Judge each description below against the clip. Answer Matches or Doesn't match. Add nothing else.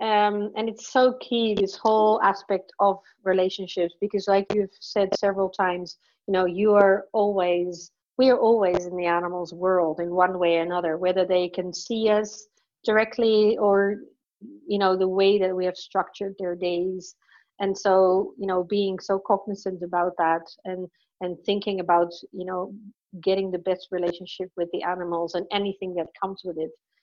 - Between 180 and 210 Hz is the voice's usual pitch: Matches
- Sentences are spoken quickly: Doesn't match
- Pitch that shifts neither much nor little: Doesn't match